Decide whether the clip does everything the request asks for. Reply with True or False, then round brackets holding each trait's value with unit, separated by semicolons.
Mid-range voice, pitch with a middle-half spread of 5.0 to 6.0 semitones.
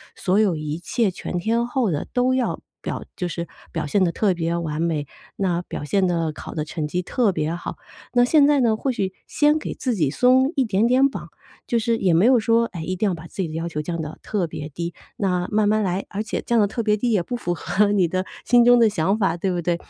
False (195 Hz; 5.5 semitones)